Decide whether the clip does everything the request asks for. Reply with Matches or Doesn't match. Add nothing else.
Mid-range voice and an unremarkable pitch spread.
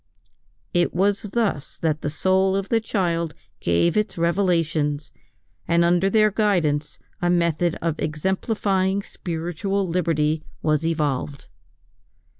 Matches